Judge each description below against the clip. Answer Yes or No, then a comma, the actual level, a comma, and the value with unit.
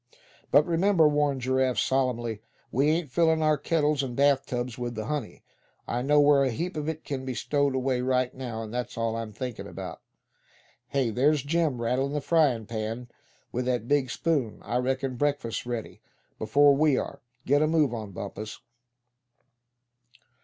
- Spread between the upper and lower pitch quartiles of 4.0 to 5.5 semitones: No, average, 3.4 semitones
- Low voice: Yes, low, 130 Hz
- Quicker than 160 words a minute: Yes, average, 170 wpm